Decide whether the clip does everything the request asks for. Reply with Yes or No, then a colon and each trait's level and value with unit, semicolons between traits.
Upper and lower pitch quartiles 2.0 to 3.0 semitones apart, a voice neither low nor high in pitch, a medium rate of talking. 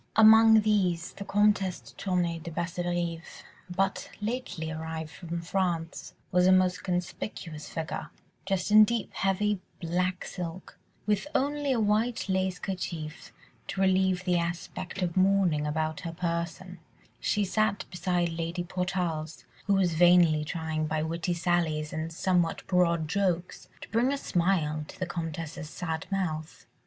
Yes: average, 2.7 semitones; medium, 180 Hz; average, 145 wpm